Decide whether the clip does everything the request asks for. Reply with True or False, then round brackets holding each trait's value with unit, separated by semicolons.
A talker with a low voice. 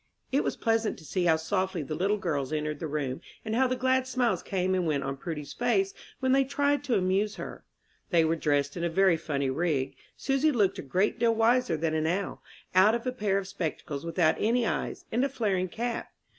False (190 Hz)